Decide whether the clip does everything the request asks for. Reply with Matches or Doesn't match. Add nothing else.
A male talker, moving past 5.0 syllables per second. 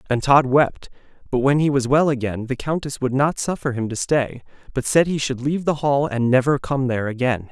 Matches